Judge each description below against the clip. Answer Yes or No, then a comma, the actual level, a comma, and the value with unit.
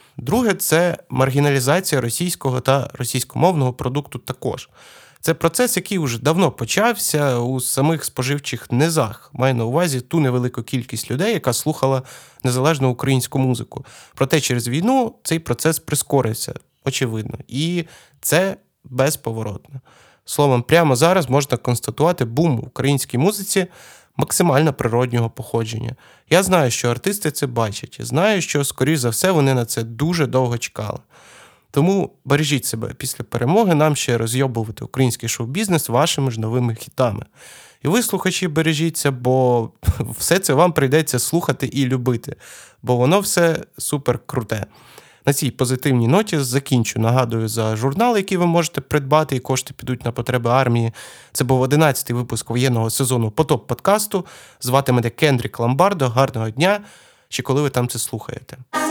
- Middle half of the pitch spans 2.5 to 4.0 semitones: No, average, 4.4 semitones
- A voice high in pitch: No, low, 135 Hz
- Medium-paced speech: Yes, average, 140 wpm